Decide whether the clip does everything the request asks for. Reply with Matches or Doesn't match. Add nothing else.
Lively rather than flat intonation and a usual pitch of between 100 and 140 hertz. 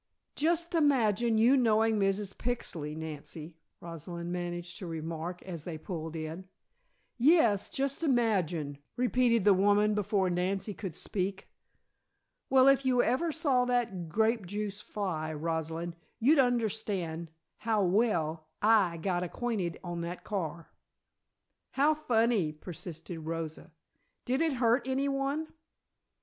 Doesn't match